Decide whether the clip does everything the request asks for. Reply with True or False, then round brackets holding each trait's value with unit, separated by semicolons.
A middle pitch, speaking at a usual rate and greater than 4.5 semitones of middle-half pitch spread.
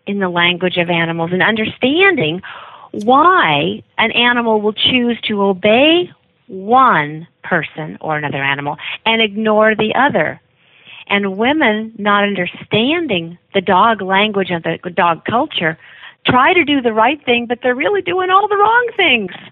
False (215 Hz; 150 wpm; 5.3 semitones)